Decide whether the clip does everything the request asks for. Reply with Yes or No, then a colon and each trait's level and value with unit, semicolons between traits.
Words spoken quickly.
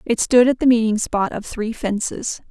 Yes: fast, 215 wpm